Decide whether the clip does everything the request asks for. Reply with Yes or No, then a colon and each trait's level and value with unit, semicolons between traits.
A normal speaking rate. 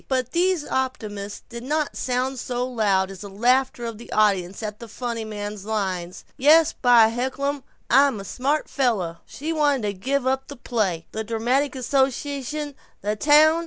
Yes: average, 165 wpm